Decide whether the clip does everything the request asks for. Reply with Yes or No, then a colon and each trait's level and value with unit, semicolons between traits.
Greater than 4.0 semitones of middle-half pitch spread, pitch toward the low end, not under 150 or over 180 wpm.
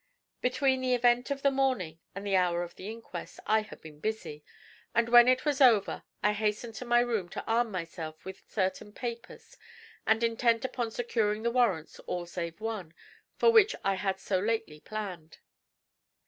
No: average, 4.4 semitones; high, 220 Hz; average, 175 wpm